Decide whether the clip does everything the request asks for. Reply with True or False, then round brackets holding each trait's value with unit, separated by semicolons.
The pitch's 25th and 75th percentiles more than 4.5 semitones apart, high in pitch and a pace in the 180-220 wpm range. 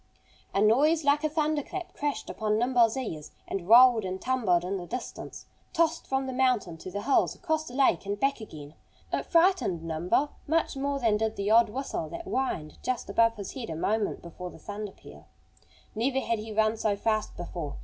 True (5.6 semitones; 225 Hz; 200 wpm)